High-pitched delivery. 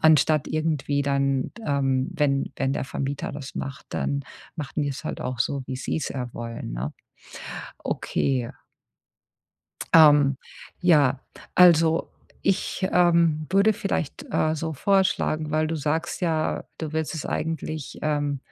No: medium, 150 Hz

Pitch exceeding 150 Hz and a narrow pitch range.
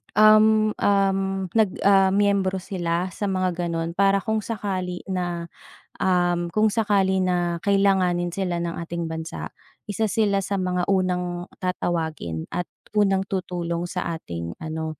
Yes: medium, 185 Hz; narrow, 2.3 semitones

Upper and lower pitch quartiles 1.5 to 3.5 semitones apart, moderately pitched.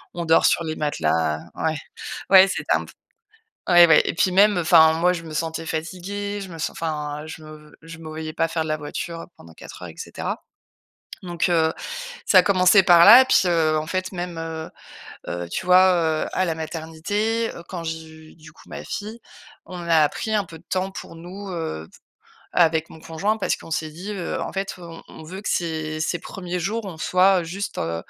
Yes: average, 2.8 semitones; medium, 165 Hz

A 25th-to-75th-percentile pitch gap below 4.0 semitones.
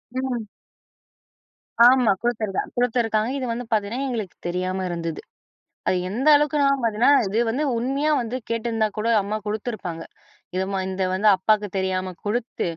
No: average, 4.3 semitones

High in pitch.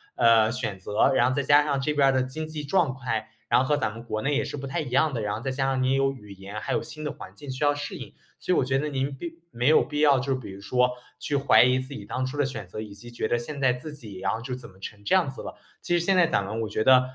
No: low, 130 Hz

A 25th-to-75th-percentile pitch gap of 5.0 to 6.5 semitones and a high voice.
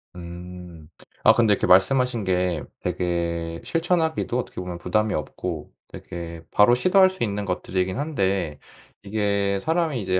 No: average, 5.3 semitones; very low, 95 Hz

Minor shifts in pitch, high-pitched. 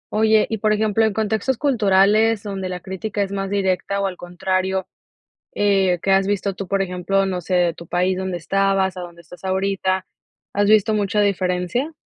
Yes: narrow, 1.8 semitones; high, 195 Hz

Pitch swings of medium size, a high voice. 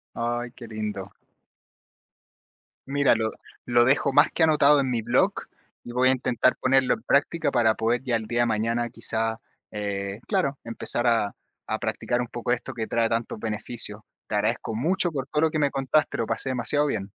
No: average, 3.1 semitones; low, 120 Hz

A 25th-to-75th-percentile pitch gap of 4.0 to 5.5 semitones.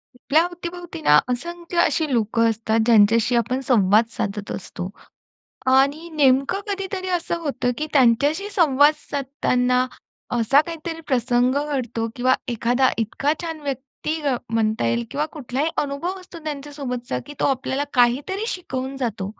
Yes: average, 4.6 semitones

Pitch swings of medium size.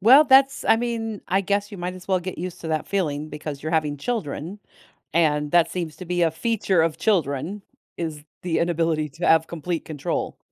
Yes: average, 4.2 semitones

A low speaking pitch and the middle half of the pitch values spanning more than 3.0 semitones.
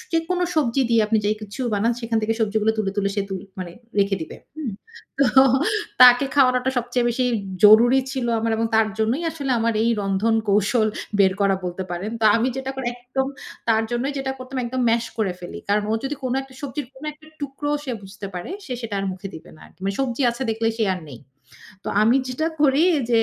No: high, 230 Hz; average, 4.1 semitones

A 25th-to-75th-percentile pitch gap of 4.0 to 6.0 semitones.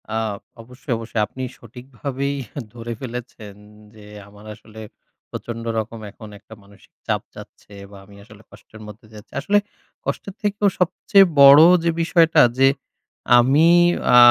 Yes: average, 4.4 semitones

